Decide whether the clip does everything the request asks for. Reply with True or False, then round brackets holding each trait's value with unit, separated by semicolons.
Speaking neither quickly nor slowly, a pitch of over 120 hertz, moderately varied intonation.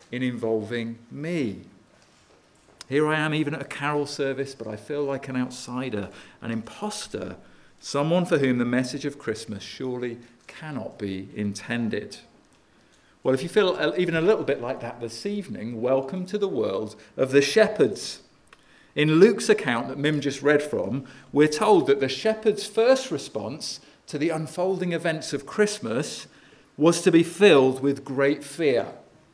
True (155 wpm; 140 Hz; 4.9 semitones)